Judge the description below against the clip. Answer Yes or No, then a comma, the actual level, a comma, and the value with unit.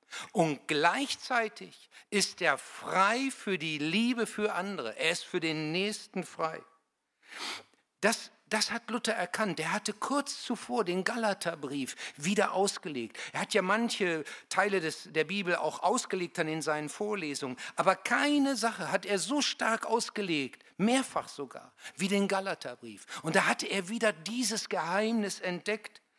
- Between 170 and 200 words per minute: No, average, 145 wpm